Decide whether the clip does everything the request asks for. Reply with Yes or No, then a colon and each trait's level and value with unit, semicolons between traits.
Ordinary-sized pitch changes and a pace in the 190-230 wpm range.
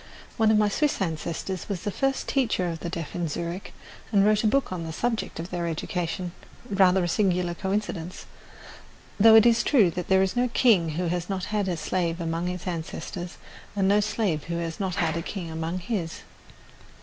Yes: average, 3.5 semitones; average, 200 wpm